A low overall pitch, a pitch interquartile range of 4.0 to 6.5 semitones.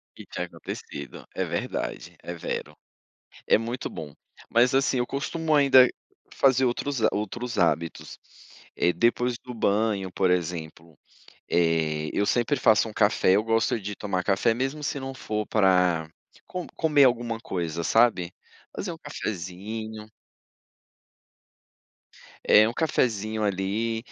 Yes: low, 110 Hz; average, 5.2 semitones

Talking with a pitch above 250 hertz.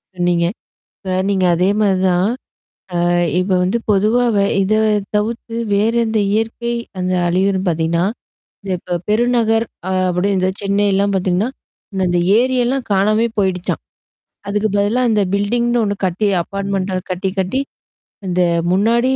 No: high, 200 Hz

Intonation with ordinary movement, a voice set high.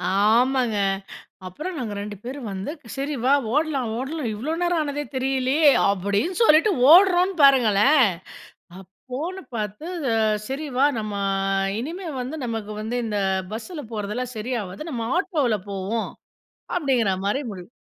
No: wide, 6.2 semitones; very high, 255 Hz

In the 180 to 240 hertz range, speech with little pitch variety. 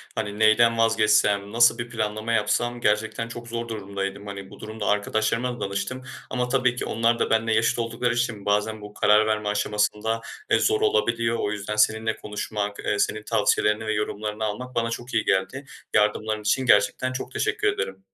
No: low, 110 Hz; narrow, 1.9 semitones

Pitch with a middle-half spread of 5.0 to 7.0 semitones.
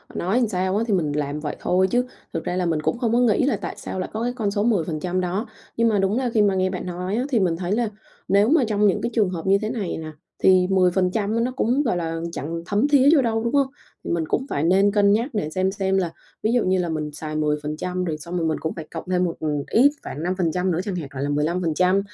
No: average, 4.6 semitones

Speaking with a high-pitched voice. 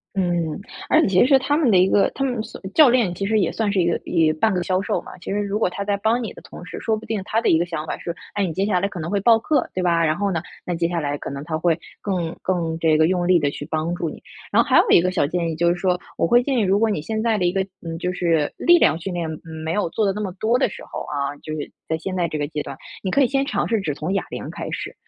No: medium, 180 Hz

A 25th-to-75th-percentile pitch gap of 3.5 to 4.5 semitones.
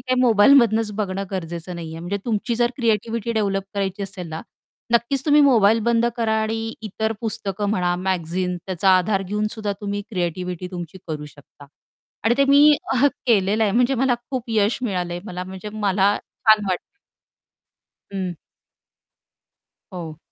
Yes: average, 3.8 semitones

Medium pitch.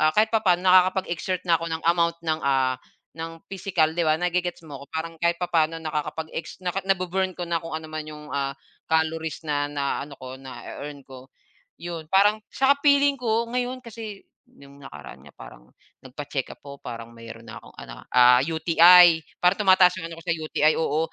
Yes: medium, 165 Hz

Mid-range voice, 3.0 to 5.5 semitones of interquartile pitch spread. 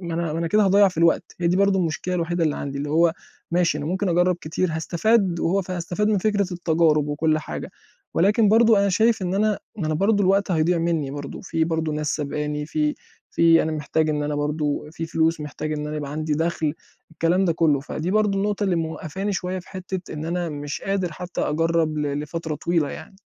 Yes: medium, 165 Hz; average, 3.5 semitones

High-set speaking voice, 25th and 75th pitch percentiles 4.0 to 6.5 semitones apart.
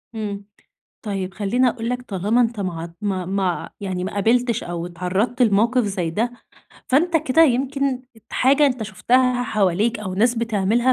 Yes: high, 220 Hz; average, 4.3 semitones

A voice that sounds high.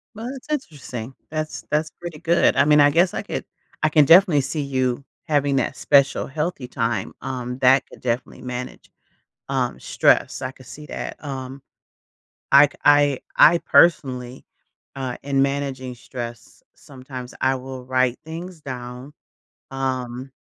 No: low, 135 Hz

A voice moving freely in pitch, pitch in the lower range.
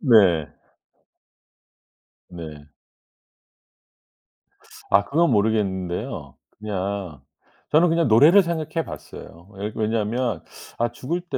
Yes: wide, 8.1 semitones; low, 110 Hz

